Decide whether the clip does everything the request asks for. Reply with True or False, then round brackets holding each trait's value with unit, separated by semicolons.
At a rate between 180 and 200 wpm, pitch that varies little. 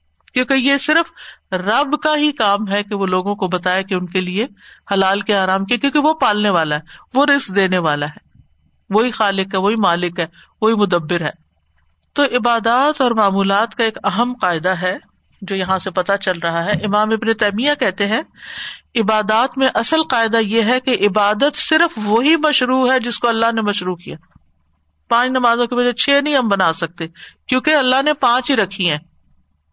False (190 wpm; 5.5 semitones)